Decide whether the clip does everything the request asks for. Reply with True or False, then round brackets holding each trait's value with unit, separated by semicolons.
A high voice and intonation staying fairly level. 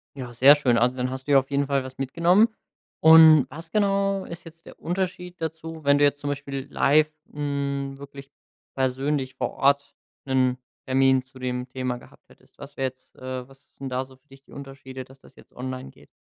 False (135 Hz; 2.3 semitones)